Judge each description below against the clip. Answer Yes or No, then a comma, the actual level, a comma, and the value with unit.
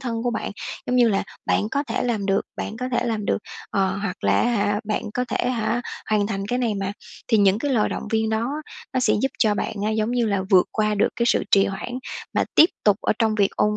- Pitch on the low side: No, high, 220 Hz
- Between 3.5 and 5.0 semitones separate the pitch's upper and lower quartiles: No, average, 2.9 semitones